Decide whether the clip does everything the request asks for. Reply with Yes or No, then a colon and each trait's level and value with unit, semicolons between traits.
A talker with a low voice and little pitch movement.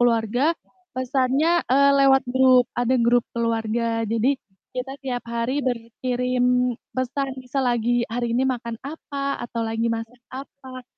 No: very high, 250 Hz; narrow, 2.1 semitones